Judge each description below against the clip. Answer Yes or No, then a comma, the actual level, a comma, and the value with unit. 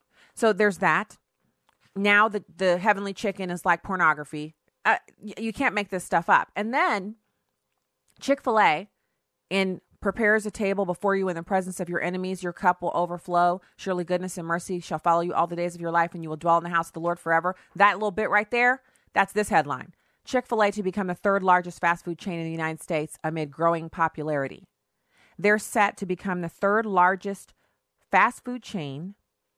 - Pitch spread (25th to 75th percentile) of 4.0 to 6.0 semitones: No, average, 3.3 semitones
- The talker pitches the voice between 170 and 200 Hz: Yes, medium, 185 Hz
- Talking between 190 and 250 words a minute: Yes, average, 200 wpm